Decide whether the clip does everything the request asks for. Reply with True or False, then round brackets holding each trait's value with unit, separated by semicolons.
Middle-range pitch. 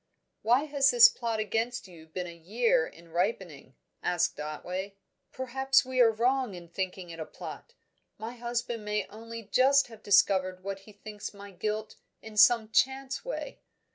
False (215 Hz)